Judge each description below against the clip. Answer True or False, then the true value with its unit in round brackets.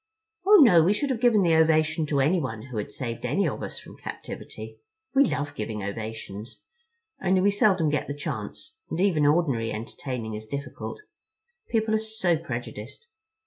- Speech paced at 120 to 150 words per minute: False (175 wpm)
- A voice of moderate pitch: True (155 Hz)